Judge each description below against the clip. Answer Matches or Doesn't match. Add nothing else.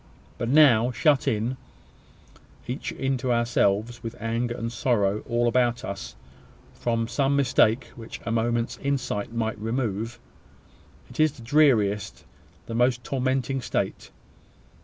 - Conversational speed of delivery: Doesn't match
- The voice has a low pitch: Matches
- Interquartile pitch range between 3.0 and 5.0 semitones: Doesn't match